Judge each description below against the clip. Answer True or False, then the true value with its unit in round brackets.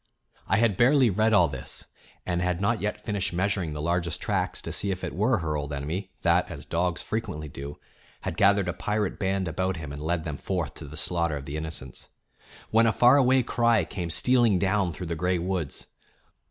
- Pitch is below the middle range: True (90 Hz)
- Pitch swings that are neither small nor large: True (4.4 semitones)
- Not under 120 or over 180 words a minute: False (205 wpm)